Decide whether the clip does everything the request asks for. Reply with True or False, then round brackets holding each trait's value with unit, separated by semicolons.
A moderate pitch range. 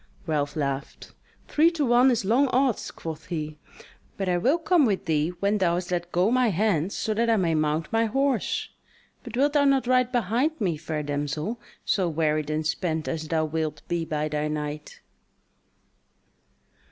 False (7.7 semitones)